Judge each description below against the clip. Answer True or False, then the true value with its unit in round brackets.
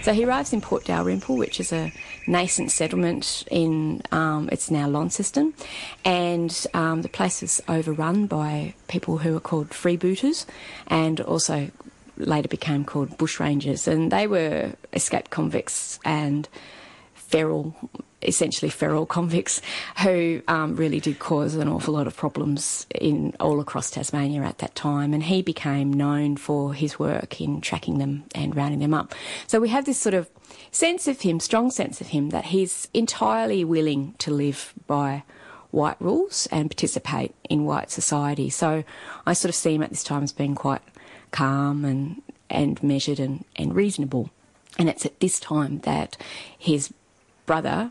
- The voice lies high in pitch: False (155 Hz)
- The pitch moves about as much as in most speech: True (3.6 semitones)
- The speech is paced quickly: False (165 wpm)